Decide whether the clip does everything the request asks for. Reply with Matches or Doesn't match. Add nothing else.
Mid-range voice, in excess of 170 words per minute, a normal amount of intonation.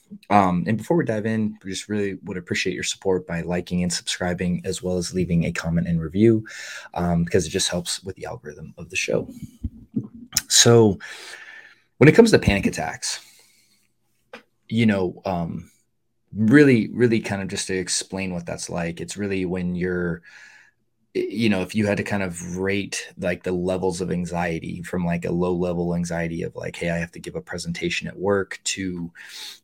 Doesn't match